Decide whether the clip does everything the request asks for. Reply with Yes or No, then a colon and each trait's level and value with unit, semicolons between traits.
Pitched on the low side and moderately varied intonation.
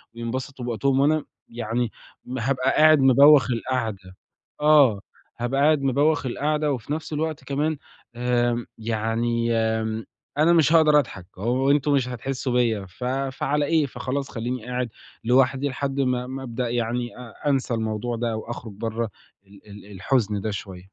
Yes: low, 125 Hz; average, 3.5 semitones